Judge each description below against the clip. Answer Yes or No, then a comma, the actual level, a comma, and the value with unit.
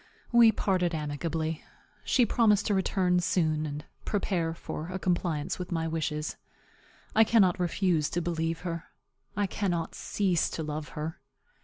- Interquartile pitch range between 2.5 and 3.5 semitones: Yes, average, 3.0 semitones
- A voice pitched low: No, medium, 170 Hz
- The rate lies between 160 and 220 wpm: No, average, 145 wpm